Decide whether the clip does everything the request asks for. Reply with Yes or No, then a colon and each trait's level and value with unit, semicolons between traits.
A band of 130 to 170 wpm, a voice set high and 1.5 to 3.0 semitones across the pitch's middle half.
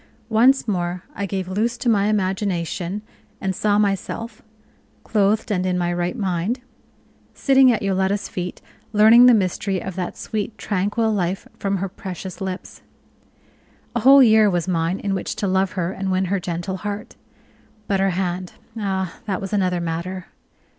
Yes: average, 160 wpm; high, 195 Hz; narrow, 2.5 semitones